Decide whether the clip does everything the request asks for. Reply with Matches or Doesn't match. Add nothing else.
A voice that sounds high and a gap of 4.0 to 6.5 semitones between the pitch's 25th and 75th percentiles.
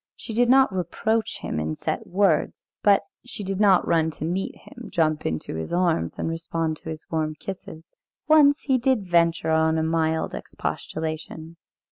Doesn't match